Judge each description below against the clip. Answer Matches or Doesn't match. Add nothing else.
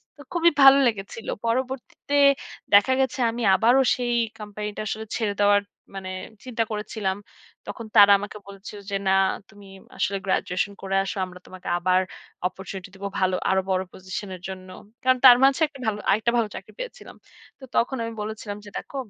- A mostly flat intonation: Doesn't match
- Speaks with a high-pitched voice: Matches